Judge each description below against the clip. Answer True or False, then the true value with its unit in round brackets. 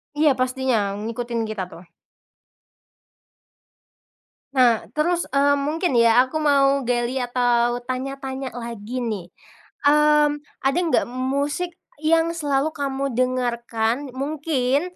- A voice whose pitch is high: True (260 Hz)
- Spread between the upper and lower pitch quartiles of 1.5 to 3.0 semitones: False (3.4 semitones)